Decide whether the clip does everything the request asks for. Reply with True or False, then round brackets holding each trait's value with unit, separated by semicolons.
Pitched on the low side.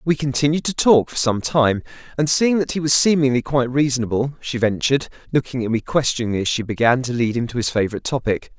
True (130 Hz)